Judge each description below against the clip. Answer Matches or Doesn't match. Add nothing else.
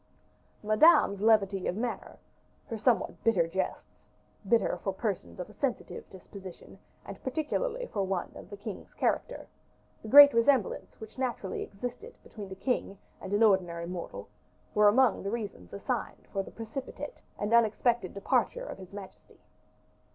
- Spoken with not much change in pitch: Doesn't match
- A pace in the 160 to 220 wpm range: Doesn't match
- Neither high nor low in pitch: Doesn't match